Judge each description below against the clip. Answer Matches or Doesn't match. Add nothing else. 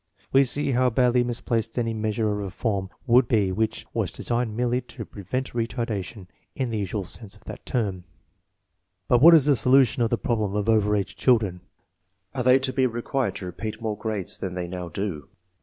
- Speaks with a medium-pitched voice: Doesn't match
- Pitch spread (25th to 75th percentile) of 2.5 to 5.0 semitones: Matches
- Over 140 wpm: Matches